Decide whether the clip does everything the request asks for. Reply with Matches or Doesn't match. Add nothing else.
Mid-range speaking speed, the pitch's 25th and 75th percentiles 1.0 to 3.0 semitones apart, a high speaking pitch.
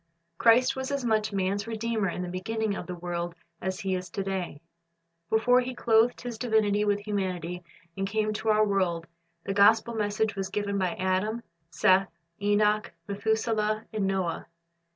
Matches